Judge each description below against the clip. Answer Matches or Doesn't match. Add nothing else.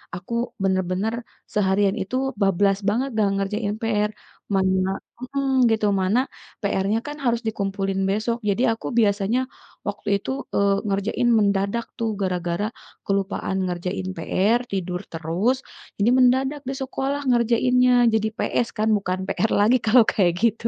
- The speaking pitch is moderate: Doesn't match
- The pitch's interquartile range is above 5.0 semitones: Doesn't match